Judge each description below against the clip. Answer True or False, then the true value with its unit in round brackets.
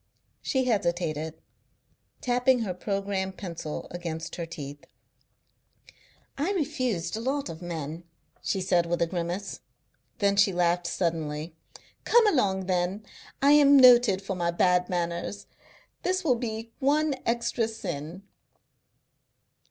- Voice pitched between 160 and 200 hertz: True (190 Hz)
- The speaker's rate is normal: False (125 wpm)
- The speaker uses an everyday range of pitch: False (5.8 semitones)